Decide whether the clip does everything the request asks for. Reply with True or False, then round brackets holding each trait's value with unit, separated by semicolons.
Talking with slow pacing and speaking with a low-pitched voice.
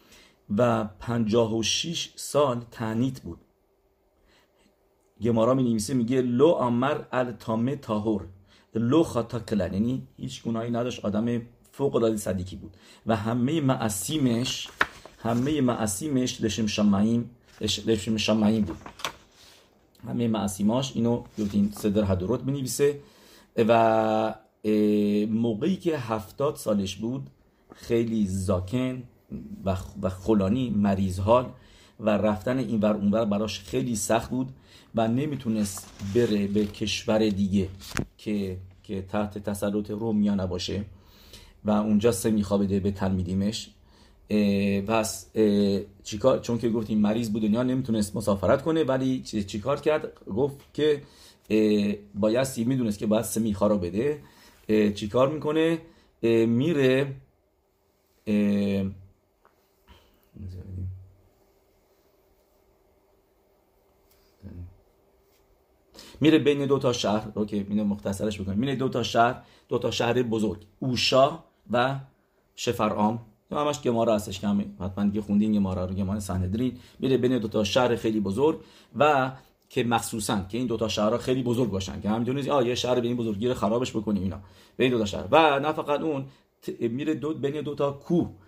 True (130 wpm; 110 Hz)